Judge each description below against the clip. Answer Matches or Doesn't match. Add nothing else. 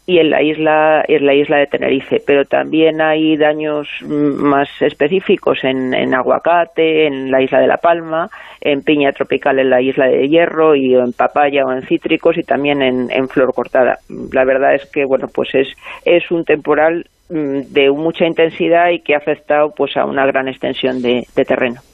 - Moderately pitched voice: Matches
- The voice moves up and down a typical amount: Matches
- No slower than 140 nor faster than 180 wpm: Doesn't match